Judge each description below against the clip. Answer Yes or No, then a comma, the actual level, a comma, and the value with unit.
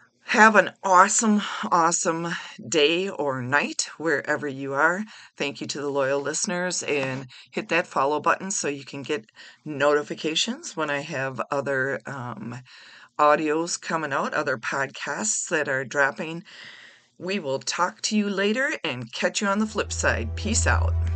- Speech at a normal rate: Yes, average, 155 wpm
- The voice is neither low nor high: Yes, medium, 155 Hz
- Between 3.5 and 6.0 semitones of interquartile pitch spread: Yes, average, 5.2 semitones